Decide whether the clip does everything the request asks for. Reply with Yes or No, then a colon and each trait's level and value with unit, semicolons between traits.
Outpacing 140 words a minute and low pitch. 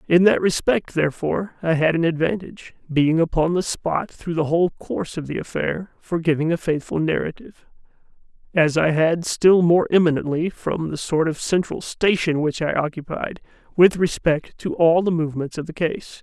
No: average, 175 wpm; medium, 165 Hz